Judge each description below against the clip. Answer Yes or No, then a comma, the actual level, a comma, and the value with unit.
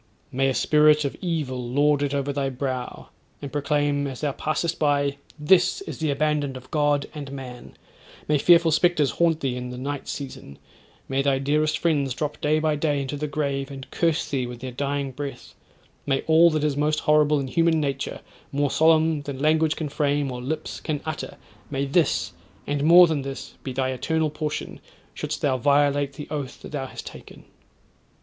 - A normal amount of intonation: No, narrow, 2.0 semitones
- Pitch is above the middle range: No, medium, 145 Hz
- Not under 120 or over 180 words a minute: No, average, 190 wpm